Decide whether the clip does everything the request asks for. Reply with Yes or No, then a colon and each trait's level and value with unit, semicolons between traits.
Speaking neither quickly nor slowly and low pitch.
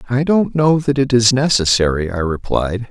Yes: average, 185 wpm; low, 120 Hz